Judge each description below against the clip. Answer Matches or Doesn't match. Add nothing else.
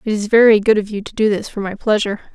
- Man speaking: Doesn't match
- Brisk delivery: Matches